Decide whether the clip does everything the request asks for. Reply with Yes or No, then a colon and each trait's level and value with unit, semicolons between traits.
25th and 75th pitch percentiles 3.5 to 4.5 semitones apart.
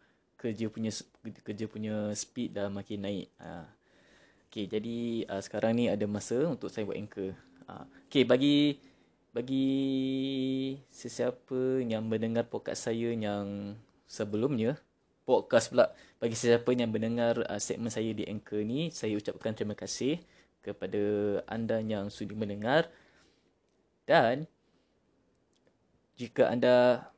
No: average, 2.9 semitones